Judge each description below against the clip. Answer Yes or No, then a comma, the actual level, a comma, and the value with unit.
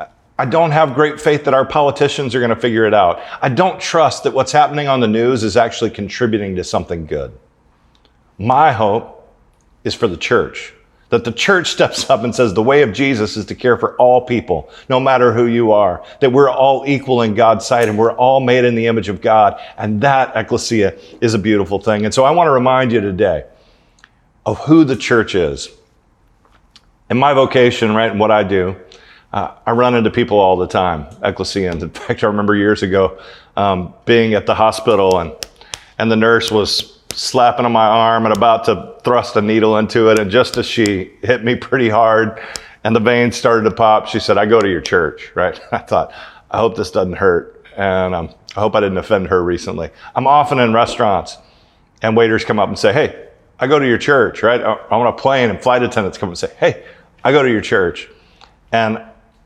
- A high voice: No, low, 115 Hz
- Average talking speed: No, fast, 210 wpm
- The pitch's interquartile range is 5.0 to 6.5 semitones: No, average, 2.8 semitones